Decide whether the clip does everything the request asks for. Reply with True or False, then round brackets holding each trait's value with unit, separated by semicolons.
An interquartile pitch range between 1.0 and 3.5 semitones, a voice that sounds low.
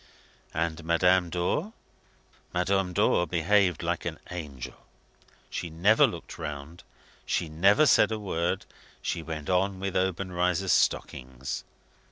True (2.8 semitones; 90 Hz)